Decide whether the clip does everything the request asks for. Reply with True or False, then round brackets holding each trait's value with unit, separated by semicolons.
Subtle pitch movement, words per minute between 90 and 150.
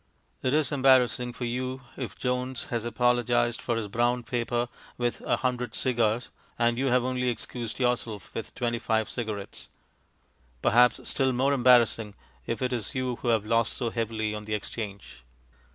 False (1.8 semitones; 165 wpm)